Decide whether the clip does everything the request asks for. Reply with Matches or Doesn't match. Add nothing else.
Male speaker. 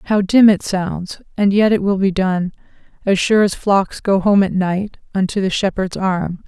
Doesn't match